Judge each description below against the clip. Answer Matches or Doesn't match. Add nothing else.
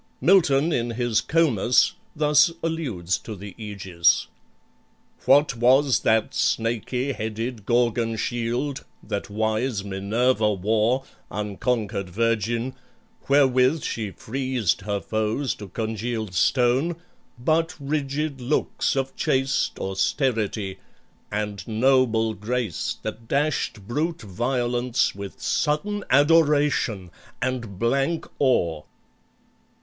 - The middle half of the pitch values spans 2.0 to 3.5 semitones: Doesn't match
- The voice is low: Matches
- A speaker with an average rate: Doesn't match